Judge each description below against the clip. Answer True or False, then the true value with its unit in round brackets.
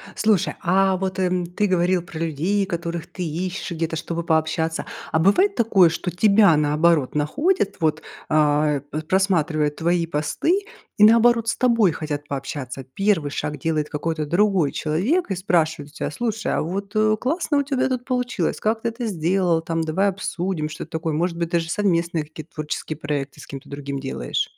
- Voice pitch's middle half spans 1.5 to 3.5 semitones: False (4.4 semitones)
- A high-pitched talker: False (170 Hz)